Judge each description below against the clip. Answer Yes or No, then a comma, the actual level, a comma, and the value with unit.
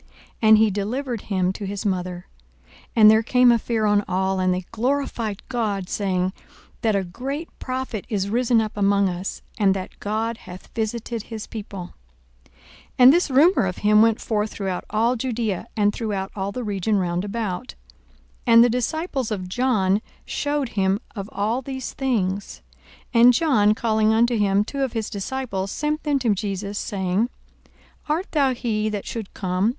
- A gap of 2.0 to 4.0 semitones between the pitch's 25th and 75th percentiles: Yes, average, 3.7 semitones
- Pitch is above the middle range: Yes, high, 215 Hz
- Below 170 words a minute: No, average, 175 wpm